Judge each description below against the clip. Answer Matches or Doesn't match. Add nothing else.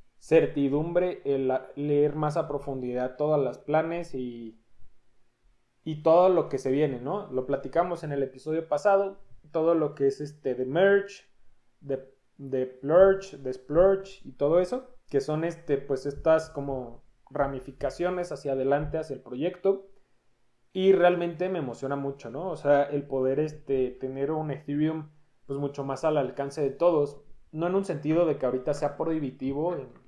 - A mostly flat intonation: Doesn't match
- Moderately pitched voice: Matches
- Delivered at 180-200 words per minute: Doesn't match